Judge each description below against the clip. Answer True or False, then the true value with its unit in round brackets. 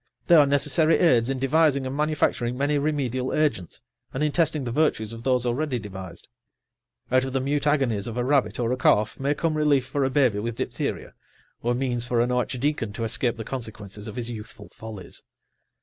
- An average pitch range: True (3.8 semitones)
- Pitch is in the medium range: False (130 Hz)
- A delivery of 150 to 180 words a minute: False (195 wpm)